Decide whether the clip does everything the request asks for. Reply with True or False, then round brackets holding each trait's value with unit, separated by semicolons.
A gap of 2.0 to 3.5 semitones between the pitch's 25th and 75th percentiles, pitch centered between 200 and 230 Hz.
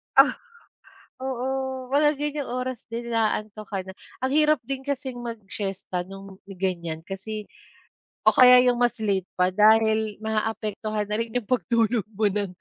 False (4.0 semitones; 220 Hz)